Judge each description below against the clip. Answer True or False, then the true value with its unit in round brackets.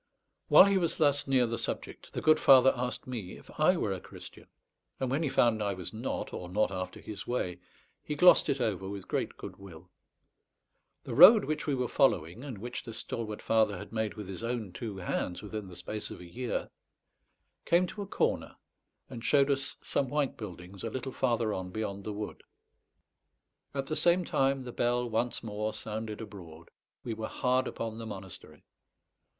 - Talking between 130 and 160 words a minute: False (190 wpm)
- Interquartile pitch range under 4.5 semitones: False (4.9 semitones)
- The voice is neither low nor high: False (115 Hz)